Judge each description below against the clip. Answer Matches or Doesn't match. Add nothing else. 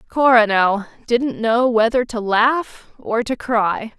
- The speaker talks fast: Doesn't match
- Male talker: Doesn't match